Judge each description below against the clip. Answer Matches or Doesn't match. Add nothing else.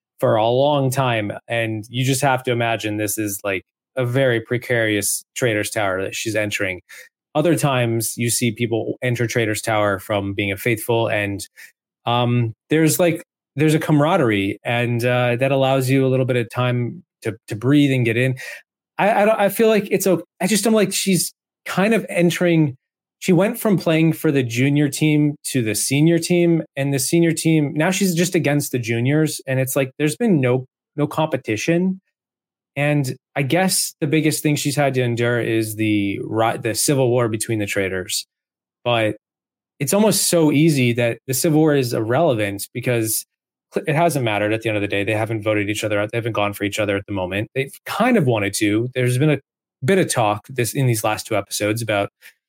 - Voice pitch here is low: Matches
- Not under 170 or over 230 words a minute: Matches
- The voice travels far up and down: Matches